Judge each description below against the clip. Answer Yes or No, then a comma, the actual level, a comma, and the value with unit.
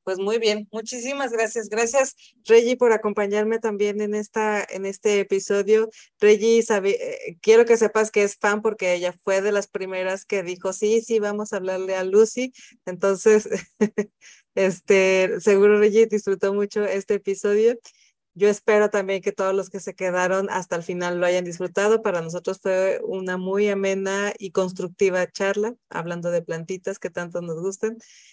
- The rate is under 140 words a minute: No, average, 165 wpm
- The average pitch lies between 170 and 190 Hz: No, high, 205 Hz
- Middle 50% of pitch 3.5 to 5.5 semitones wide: No, narrow, 2.4 semitones